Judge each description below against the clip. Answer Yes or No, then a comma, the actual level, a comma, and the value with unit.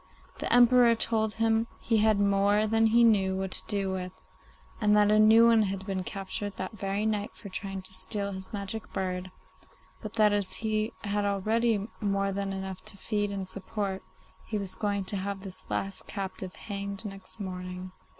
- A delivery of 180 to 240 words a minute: Yes, average, 185 wpm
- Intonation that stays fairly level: Yes, narrow, 2.0 semitones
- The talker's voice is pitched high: Yes, high, 200 Hz